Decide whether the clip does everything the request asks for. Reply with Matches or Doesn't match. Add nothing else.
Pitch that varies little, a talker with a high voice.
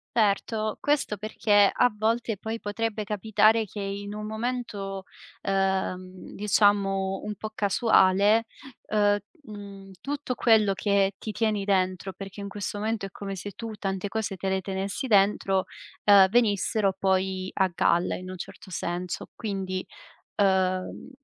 Matches